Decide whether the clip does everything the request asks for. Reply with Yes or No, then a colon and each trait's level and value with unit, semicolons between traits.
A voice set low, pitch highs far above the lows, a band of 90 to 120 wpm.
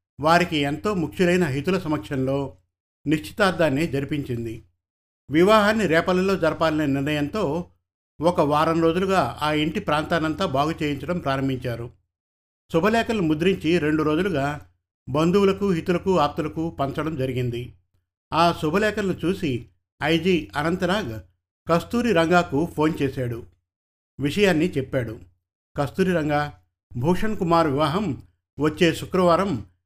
No: medium, 150 Hz; wide, 6.0 semitones; average, 95 wpm